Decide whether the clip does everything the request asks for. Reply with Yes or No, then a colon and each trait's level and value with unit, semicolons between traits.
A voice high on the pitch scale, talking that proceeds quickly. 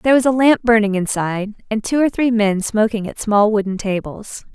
Yes: high, 215 Hz; fast, 210 wpm